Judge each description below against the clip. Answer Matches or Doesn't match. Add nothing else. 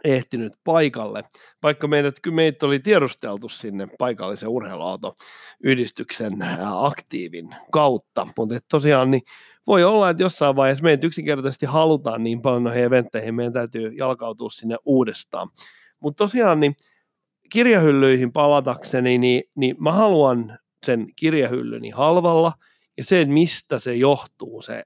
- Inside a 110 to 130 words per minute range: Matches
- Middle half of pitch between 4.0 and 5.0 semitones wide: Matches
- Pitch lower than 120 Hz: Doesn't match